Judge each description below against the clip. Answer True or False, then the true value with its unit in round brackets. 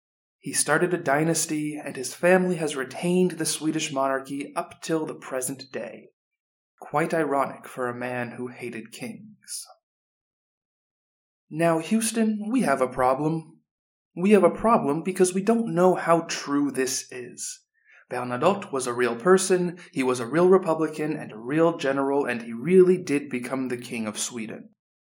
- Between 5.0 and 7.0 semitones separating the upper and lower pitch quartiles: True (5.6 semitones)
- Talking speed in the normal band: True (160 wpm)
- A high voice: False (155 Hz)